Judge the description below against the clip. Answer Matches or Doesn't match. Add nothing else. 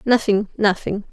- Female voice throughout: Matches